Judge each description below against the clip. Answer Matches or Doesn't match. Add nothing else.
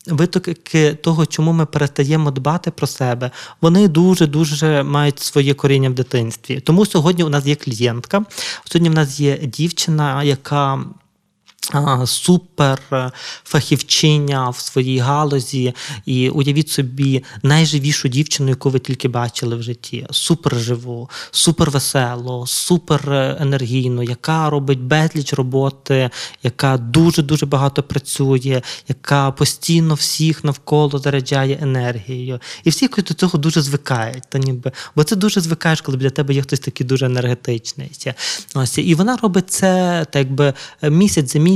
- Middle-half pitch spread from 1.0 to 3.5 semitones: Matches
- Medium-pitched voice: Matches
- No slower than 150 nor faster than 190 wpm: Doesn't match